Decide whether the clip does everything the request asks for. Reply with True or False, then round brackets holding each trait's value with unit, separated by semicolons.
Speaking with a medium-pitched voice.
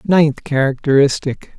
True (145 Hz)